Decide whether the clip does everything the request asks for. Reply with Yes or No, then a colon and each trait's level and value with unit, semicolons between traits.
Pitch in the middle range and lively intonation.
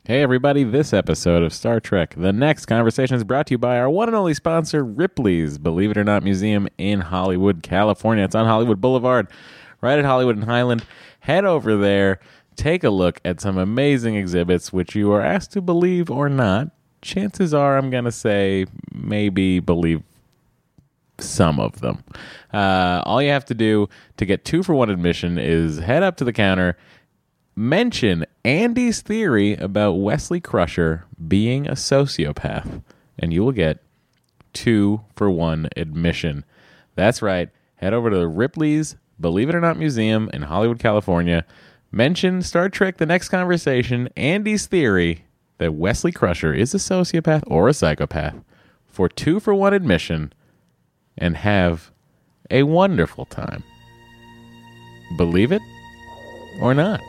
No: low, 115 Hz; wide, 7.4 semitones